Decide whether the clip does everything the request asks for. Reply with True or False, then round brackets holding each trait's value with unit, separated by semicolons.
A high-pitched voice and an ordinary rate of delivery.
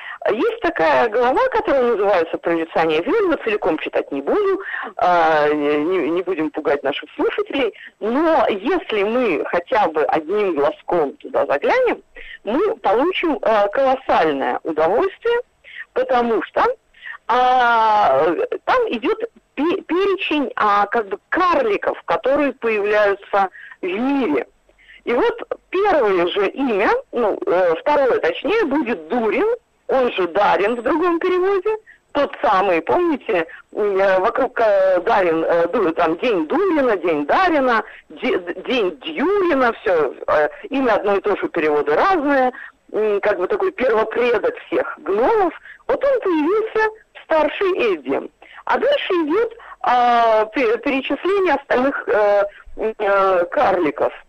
False (315 Hz; 105 wpm)